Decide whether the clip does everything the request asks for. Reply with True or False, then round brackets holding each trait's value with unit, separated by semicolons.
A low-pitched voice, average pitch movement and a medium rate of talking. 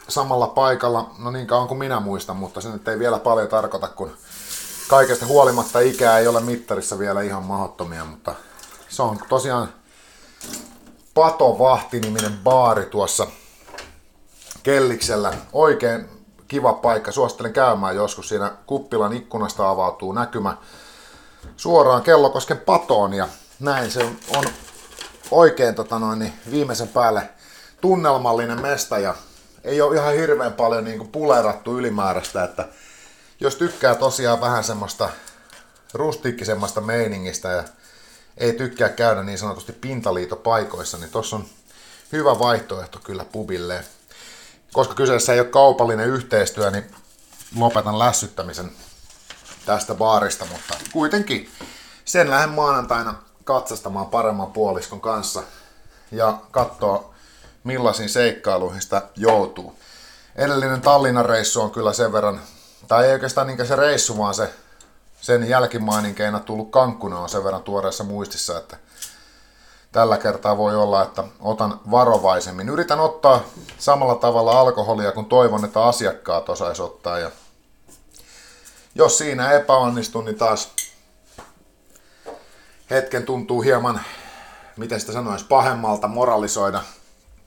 True (115 Hz; 3.9 semitones; 120 wpm)